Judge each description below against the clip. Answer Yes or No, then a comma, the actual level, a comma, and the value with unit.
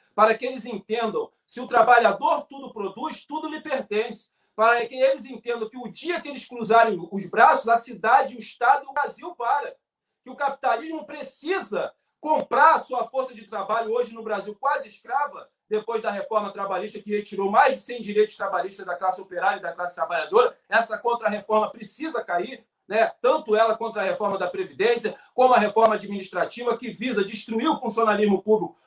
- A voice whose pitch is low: No, high, 230 Hz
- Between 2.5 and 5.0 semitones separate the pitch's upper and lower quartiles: Yes, average, 4.7 semitones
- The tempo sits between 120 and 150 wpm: No, average, 180 wpm